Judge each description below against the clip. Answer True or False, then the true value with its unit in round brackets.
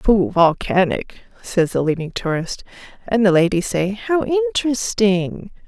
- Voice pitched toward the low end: False (190 Hz)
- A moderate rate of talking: False (125 wpm)